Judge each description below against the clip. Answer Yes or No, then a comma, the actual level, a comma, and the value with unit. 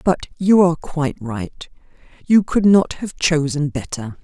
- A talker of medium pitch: Yes, medium, 160 Hz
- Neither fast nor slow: Yes, average, 155 wpm